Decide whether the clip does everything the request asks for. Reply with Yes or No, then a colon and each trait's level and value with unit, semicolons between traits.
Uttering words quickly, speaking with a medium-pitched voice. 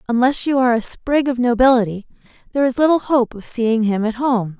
No: fast, 210 wpm; high, 245 Hz